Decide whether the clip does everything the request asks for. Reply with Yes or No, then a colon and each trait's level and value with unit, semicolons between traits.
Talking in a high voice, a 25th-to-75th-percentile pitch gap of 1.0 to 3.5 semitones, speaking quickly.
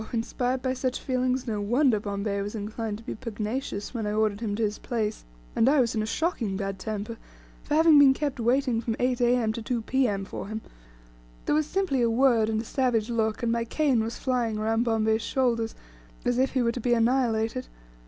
Yes: high, 230 Hz; average, 2.8 semitones; fast, 210 wpm